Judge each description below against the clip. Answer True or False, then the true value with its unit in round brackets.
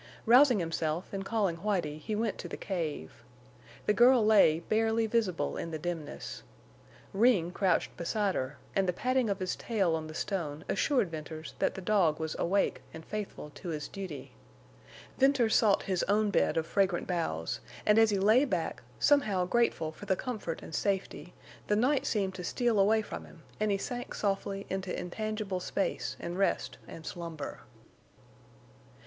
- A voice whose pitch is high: True (195 Hz)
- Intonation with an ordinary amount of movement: True (4.5 semitones)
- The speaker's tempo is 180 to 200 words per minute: False (170 wpm)